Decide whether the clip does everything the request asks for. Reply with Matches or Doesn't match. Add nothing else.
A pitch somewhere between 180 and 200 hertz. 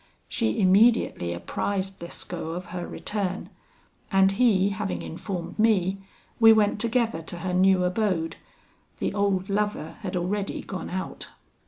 Matches